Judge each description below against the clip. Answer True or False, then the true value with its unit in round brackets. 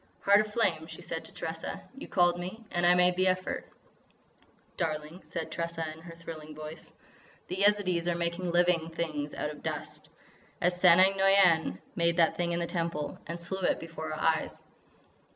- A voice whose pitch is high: False (170 Hz)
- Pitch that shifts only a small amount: True (1.9 semitones)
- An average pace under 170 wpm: False (175 wpm)